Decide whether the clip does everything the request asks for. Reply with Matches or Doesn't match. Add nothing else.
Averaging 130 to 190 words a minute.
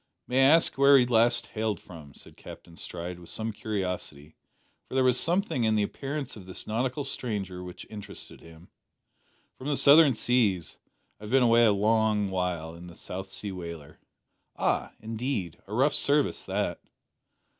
Matches